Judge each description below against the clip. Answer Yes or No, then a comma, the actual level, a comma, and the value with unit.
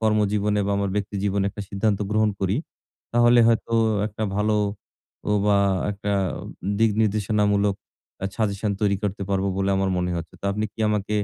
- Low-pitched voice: Yes, low, 105 Hz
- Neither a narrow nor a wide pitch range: No, narrow, 1.3 semitones